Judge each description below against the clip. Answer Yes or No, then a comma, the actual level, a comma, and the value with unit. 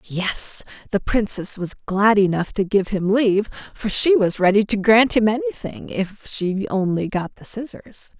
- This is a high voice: Yes, high, 210 Hz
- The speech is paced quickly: No, average, 175 wpm